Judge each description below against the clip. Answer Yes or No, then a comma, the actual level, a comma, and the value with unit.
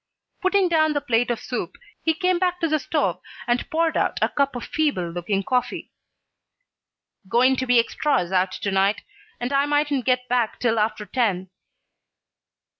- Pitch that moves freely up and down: Yes, wide, 5.7 semitones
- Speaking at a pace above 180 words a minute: No, average, 170 wpm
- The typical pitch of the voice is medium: No, very high, 250 Hz